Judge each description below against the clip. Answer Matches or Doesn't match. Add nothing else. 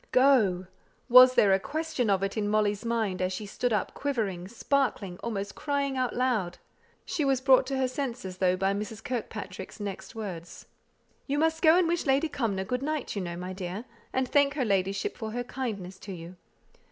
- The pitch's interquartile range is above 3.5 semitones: Matches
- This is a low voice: Doesn't match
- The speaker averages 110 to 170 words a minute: Doesn't match